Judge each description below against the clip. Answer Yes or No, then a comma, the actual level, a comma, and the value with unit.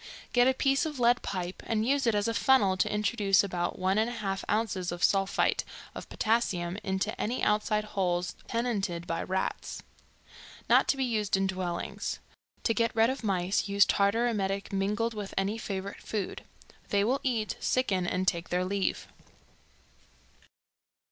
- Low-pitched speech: No, high, 205 Hz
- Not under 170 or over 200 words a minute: No, average, 160 wpm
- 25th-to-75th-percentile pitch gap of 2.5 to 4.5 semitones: Yes, average, 3.3 semitones